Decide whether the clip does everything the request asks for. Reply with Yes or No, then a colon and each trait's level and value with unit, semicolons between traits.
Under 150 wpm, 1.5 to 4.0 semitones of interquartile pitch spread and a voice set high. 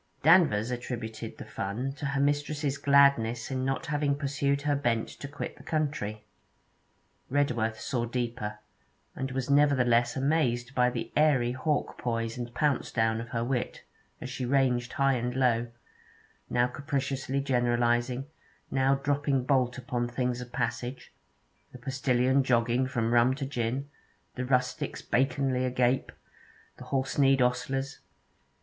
No: average, 140 wpm; narrow, 2.4 semitones; low, 130 Hz